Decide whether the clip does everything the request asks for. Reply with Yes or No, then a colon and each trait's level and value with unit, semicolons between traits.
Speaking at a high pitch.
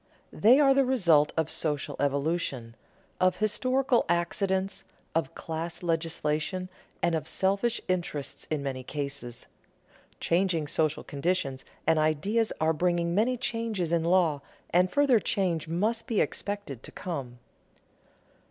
No: medium, 170 Hz